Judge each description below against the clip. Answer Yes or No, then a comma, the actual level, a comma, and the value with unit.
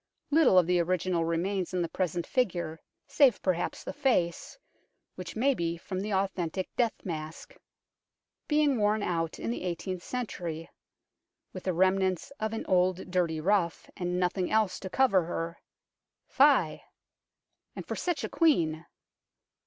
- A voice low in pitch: No, medium, 185 Hz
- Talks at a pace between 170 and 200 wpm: No, average, 155 wpm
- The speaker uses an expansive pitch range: No, average, 3.8 semitones